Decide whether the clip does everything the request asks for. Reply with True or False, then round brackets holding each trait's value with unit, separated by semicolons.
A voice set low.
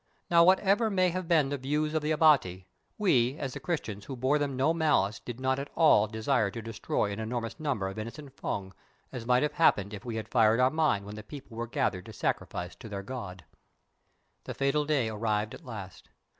True (125 Hz)